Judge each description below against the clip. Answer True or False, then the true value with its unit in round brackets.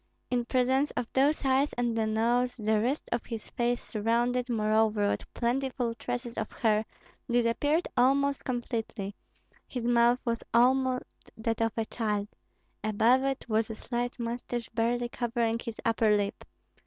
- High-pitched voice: True (235 Hz)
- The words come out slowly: False (150 wpm)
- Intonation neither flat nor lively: False (1.9 semitones)